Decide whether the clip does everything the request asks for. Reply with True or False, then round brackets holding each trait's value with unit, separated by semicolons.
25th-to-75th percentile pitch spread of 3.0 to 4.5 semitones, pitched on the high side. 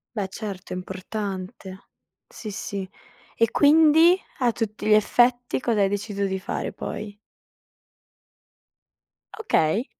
True (3.9 semitones; 210 Hz)